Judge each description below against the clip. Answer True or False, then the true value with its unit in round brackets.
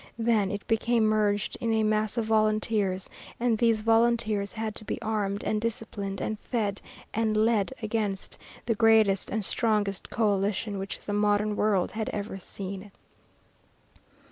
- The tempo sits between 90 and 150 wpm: True (145 wpm)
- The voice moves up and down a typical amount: False (1.6 semitones)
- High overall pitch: True (215 Hz)